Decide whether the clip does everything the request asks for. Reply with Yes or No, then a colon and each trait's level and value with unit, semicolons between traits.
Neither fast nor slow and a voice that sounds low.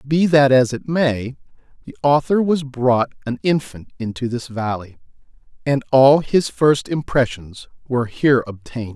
Yes: average, 145 wpm; low, 130 Hz